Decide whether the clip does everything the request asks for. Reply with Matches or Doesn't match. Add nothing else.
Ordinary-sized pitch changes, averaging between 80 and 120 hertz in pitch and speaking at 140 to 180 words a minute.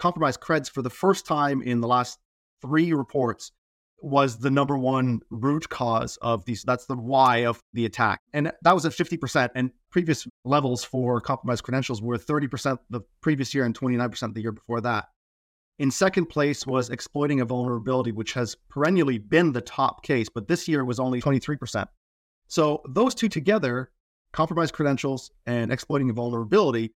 Doesn't match